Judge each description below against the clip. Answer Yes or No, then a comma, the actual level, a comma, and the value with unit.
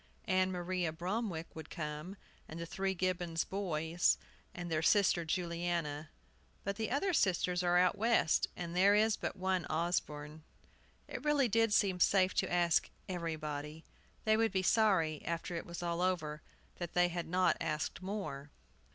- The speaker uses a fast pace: No, average, 155 wpm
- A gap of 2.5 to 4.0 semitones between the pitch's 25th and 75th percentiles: Yes, average, 2.8 semitones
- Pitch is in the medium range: Yes, medium, 175 Hz